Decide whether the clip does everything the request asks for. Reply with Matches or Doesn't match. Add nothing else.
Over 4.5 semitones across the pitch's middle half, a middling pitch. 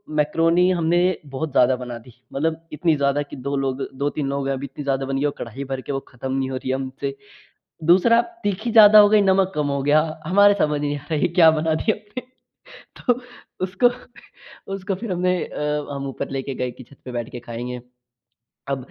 Matches